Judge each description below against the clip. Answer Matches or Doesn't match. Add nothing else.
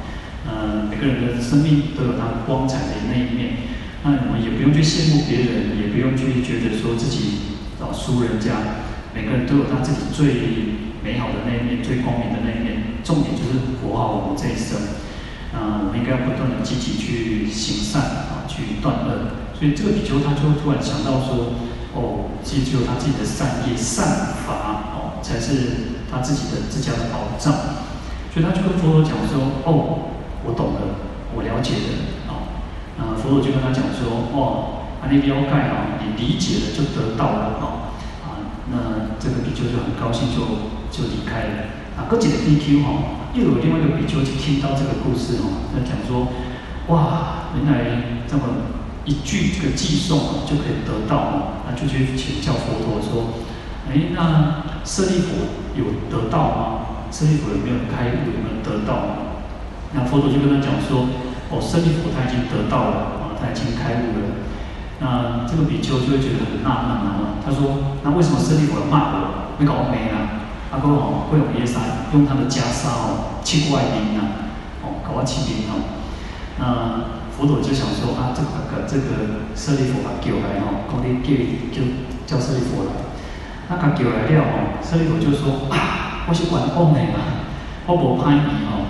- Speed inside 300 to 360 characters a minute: Doesn't match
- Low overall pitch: Matches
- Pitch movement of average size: Matches